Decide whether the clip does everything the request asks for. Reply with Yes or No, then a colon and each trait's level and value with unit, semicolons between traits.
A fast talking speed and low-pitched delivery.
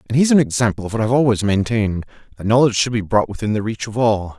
Yes: fast, 260 wpm; low, 110 Hz